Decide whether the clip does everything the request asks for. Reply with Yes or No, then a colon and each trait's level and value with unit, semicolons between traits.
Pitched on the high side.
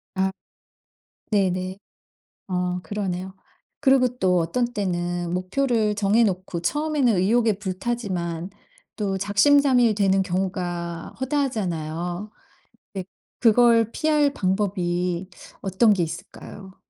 Yes: high, 195 Hz